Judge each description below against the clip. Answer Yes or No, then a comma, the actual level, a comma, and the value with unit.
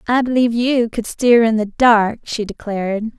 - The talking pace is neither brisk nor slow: Yes, average, 190 wpm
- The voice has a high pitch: Yes, high, 225 Hz